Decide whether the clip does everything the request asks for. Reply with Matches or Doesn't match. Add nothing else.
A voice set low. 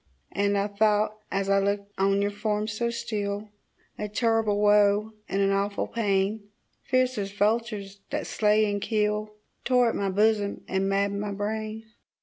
Doesn't match